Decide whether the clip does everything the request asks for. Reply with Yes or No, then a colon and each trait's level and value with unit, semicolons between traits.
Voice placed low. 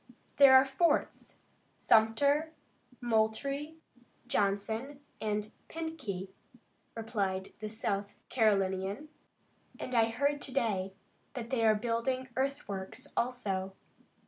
No: high, 225 Hz